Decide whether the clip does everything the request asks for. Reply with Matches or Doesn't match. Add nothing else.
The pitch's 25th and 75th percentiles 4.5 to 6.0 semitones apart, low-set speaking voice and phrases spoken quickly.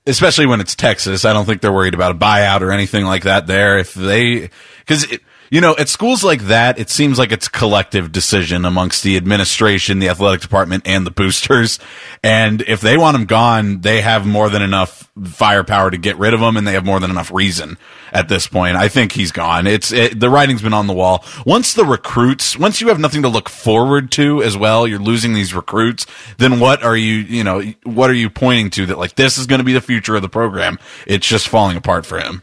Doesn't match